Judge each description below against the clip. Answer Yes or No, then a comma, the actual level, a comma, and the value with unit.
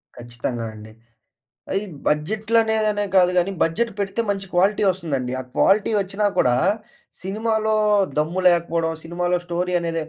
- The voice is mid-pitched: Yes, medium, 180 Hz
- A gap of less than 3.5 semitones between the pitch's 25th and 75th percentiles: No, average, 4.0 semitones